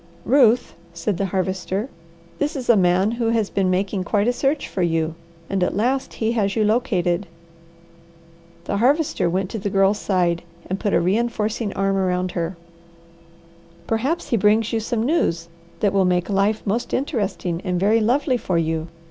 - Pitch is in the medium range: No, high, 200 Hz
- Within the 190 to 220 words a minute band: No, average, 175 wpm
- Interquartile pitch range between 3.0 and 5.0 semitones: Yes, average, 3.9 semitones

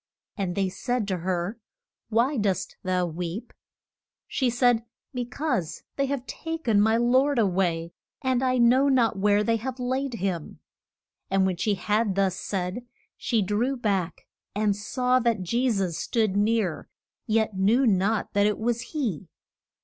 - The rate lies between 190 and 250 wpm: No, average, 160 wpm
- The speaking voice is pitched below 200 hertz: No, high, 215 Hz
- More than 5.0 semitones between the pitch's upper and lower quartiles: No, average, 4.4 semitones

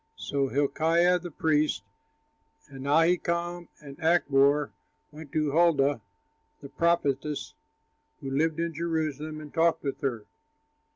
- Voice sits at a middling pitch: Yes, medium, 155 Hz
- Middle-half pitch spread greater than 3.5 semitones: No, average, 3.1 semitones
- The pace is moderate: No, slow, 115 wpm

